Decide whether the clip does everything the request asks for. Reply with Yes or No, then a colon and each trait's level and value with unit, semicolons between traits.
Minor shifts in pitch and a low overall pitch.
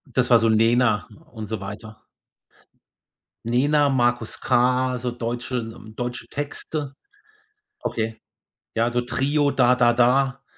Yes: narrow, 2.2 semitones; low, 120 Hz